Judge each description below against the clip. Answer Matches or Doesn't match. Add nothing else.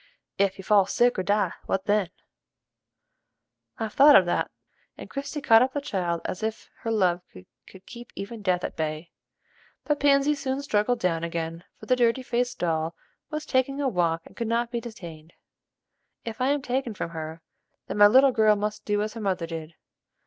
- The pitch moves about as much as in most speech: Doesn't match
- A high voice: Matches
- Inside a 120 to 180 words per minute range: Doesn't match